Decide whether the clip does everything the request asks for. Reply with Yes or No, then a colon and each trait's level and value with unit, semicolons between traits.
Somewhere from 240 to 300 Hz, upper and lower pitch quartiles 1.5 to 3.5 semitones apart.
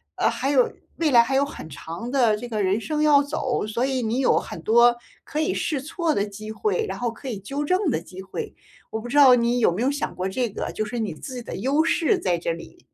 No: high, 245 Hz; average, 5.1 semitones